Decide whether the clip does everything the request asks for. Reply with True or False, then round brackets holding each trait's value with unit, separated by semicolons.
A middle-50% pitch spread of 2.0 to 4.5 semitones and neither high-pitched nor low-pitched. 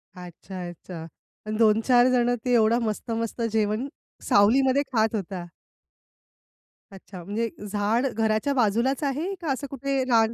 False (3.6 semitones; 225 Hz)